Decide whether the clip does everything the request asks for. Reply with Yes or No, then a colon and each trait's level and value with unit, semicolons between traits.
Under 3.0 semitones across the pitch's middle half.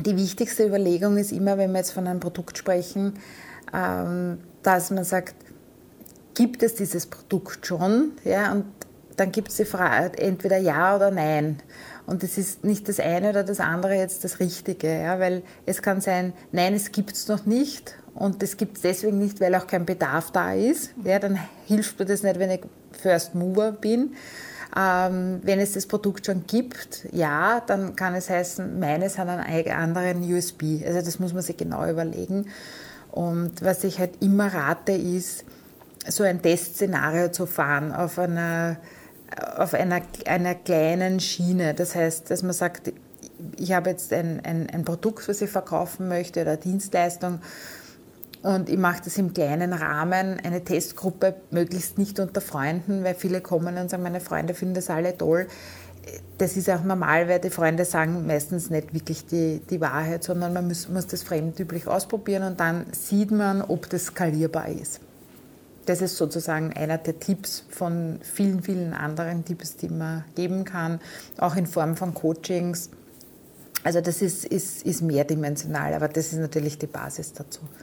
Yes: narrow, 2.4 semitones